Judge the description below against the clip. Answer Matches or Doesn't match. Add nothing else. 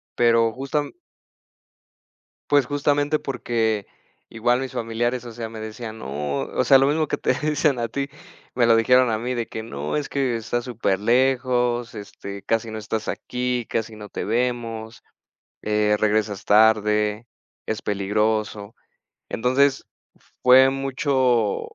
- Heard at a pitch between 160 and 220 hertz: Doesn't match